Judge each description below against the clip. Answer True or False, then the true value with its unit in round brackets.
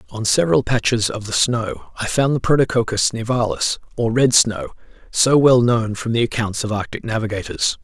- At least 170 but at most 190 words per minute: True (175 wpm)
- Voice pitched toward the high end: False (115 Hz)